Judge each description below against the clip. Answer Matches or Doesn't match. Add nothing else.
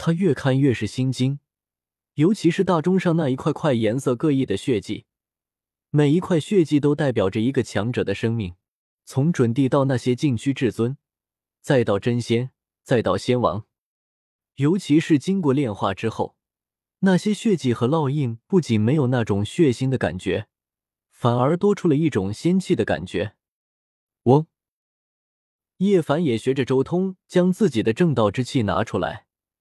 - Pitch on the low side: Matches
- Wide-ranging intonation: Matches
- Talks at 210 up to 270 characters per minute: Matches